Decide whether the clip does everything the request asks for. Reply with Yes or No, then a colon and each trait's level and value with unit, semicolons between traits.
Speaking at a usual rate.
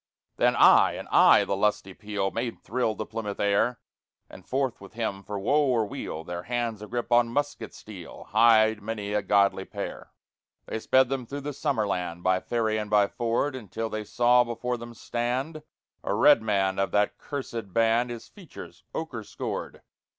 Yes: average, 180 wpm